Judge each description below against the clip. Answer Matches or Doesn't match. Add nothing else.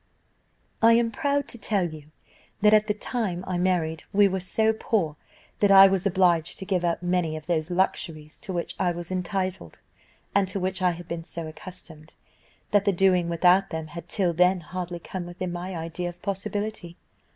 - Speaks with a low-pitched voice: Doesn't match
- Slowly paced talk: Doesn't match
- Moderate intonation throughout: Doesn't match